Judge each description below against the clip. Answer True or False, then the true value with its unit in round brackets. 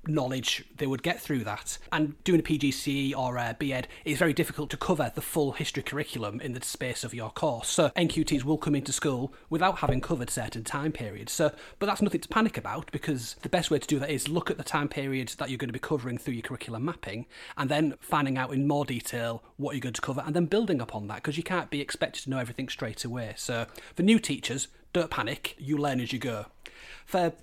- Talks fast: True (240 wpm)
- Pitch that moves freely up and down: False (3.5 semitones)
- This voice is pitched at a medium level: True (145 Hz)